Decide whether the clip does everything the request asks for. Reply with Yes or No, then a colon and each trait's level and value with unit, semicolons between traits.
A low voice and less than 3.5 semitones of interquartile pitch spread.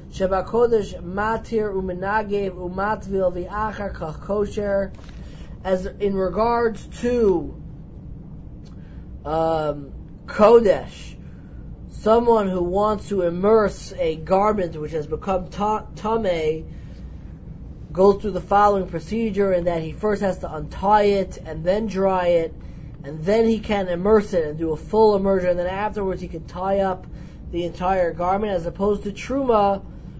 No: high, 195 Hz; average, 2.9 semitones